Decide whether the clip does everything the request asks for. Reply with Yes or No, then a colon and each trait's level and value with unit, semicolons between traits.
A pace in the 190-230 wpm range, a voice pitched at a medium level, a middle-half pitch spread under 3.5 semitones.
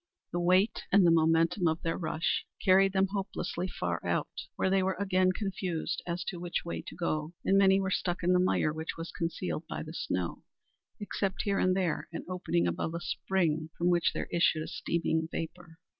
Yes: average, 200 wpm; medium, 175 Hz; narrow, 2.5 semitones